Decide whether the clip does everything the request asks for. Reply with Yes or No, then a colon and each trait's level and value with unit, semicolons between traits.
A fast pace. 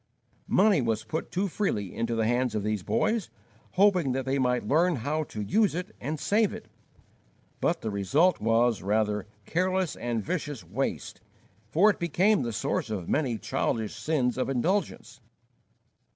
No: average, 160 wpm